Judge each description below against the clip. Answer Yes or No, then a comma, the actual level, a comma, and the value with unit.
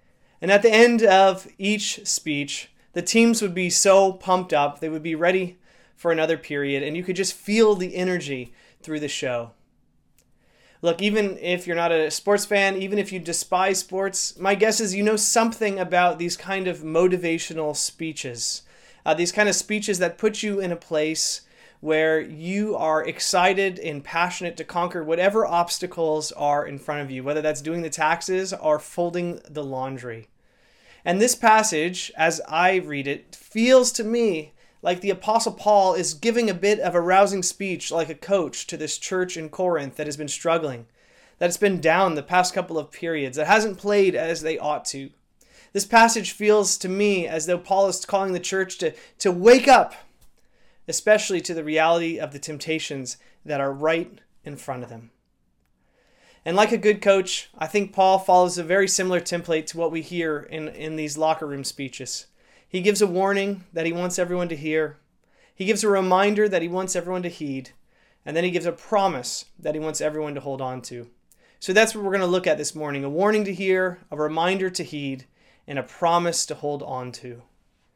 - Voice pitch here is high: No, medium, 175 Hz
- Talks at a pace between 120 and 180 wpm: No, average, 195 wpm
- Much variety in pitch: No, average, 4.1 semitones